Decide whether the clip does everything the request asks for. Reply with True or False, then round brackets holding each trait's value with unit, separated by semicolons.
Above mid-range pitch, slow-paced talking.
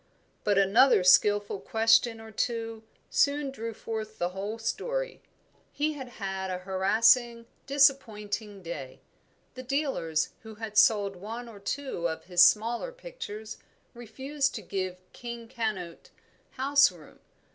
True (225 Hz; 130 wpm)